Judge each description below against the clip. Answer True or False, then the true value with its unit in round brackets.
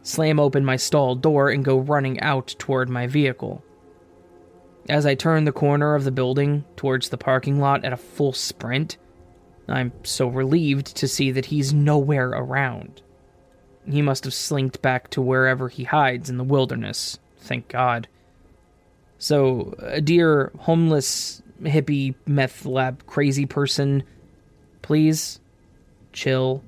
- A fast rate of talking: False (140 wpm)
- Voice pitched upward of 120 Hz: True (135 Hz)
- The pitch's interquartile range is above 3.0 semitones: False (2.5 semitones)